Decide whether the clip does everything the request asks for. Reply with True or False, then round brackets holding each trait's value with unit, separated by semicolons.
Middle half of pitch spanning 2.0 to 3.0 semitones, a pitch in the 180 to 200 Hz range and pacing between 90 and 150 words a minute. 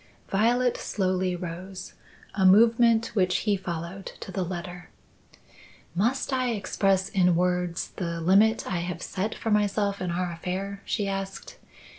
True (2.6 semitones; 190 Hz; 140 wpm)